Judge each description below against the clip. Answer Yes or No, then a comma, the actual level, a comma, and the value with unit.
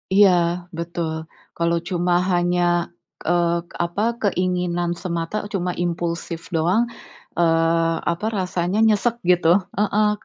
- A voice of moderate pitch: Yes, medium, 175 Hz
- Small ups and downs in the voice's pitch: Yes, narrow, 1.4 semitones